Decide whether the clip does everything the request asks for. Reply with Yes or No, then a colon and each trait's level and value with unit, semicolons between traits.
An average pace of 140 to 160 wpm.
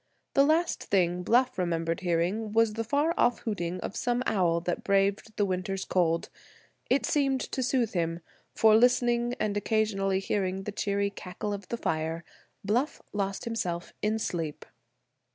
Yes: average, 155 wpm